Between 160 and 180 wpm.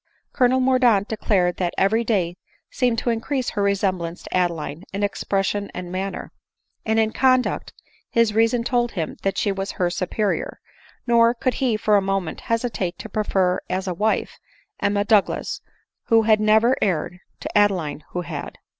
Yes: average, 165 wpm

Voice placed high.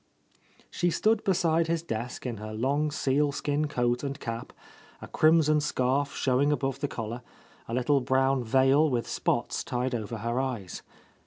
No: low, 135 Hz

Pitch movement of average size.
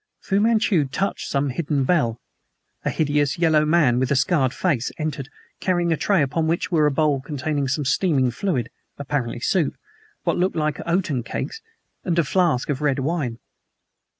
Yes: average, 4.1 semitones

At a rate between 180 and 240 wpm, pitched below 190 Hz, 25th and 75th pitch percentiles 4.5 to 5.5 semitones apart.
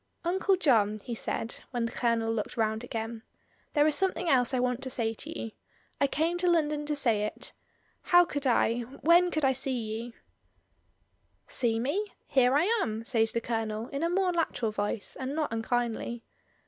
No: average, 185 wpm; very high, 250 Hz; average, 5.1 semitones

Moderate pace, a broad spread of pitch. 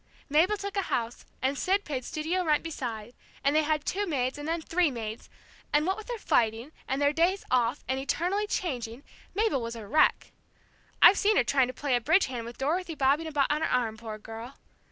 No: fast, 215 wpm; wide, 5.7 semitones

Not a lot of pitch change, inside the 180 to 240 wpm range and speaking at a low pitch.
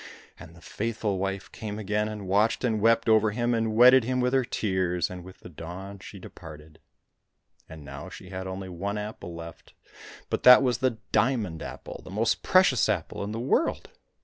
No: average, 3.8 semitones; average, 190 wpm; low, 105 Hz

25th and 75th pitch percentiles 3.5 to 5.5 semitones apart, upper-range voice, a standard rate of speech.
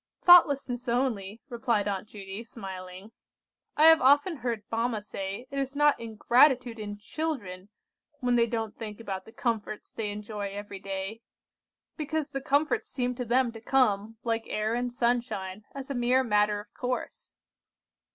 Yes: average, 3.8 semitones; high, 230 Hz; average, 155 wpm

